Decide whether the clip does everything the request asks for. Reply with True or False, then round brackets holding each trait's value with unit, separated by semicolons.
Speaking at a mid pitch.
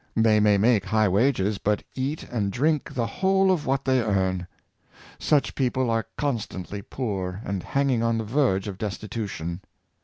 False (110 Hz)